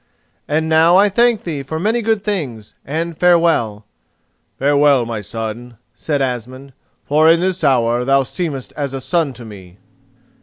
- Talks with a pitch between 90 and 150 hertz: Yes, medium, 140 Hz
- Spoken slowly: No, average, 155 wpm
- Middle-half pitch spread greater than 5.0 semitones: Yes, wide, 5.6 semitones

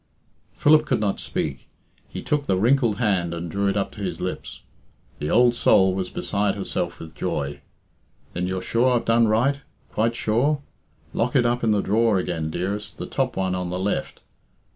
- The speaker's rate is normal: Yes, average, 185 wpm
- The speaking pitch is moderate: No, low, 105 Hz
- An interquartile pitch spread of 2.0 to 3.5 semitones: No, average, 4.4 semitones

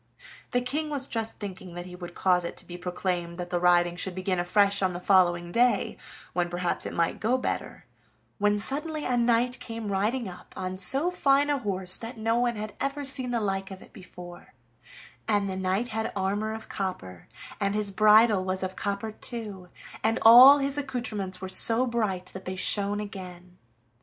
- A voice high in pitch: Yes, high, 200 Hz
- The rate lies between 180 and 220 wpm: Yes, average, 190 wpm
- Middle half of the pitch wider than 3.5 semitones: Yes, average, 4.3 semitones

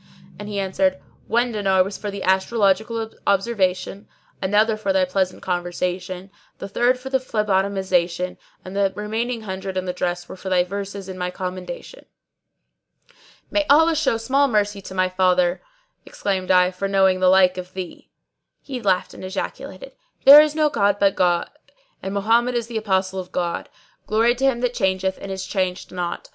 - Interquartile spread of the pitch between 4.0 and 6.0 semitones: No, average, 3.2 semitones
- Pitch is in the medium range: No, high, 195 Hz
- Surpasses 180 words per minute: No, average, 175 wpm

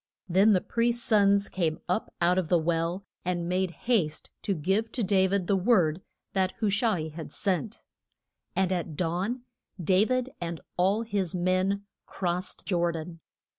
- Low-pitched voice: No, medium, 185 Hz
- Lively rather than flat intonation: No, average, 2.7 semitones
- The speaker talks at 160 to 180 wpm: Yes, average, 170 wpm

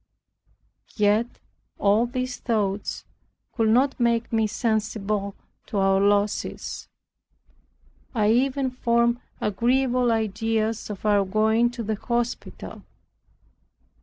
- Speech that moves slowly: Yes, slow, 100 wpm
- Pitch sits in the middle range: No, high, 225 Hz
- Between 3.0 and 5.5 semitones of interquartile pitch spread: No, narrow, 2.5 semitones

